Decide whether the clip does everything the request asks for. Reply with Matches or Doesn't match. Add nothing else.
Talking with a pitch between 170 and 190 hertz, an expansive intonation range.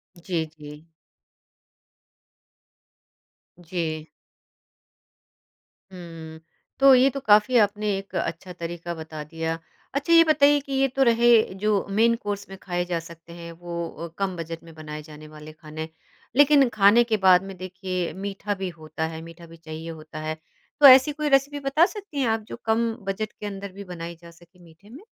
Matches